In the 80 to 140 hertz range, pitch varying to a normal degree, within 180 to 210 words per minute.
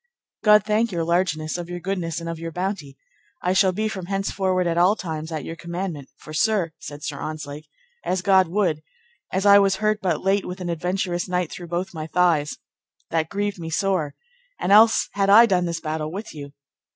No: medium, 180 Hz; average, 3.2 semitones; average, 200 wpm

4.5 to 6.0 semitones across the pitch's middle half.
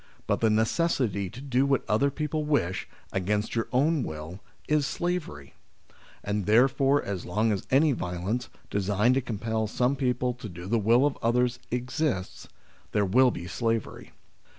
Yes: average, 4.8 semitones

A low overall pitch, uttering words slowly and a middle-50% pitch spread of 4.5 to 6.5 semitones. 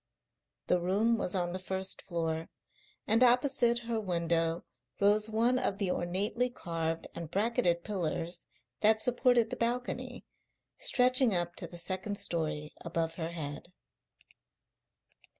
No: medium, 185 Hz; slow, 130 wpm; average, 5.2 semitones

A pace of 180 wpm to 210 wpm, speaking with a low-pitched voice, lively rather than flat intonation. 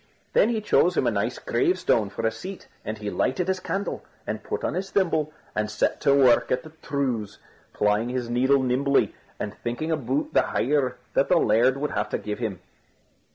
Yes: average, 200 wpm; low, 130 Hz; wide, 5.9 semitones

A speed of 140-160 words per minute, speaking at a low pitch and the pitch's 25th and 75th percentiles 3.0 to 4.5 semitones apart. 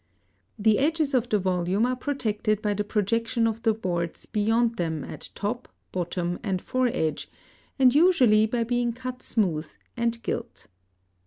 No: average, 155 wpm; high, 225 Hz; average, 4.1 semitones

